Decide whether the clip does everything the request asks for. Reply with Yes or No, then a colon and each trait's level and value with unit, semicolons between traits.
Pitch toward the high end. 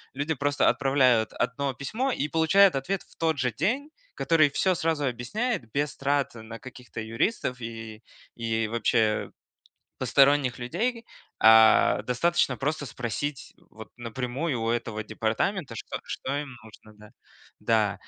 No: low, 130 Hz